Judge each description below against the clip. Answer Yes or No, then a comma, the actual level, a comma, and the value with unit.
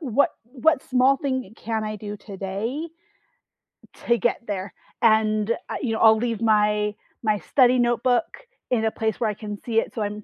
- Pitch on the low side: No, high, 220 Hz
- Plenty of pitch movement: No, average, 2.7 semitones